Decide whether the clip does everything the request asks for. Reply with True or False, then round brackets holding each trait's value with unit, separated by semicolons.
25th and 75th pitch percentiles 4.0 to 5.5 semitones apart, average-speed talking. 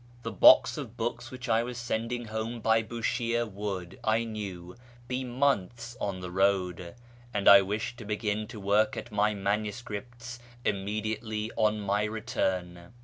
False (2.7 semitones; 150 wpm)